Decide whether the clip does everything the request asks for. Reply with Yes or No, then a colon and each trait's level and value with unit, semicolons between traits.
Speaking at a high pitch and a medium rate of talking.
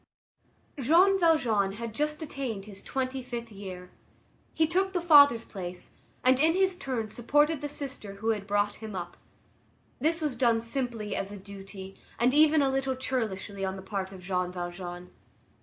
Yes: high, 230 Hz; average, 170 wpm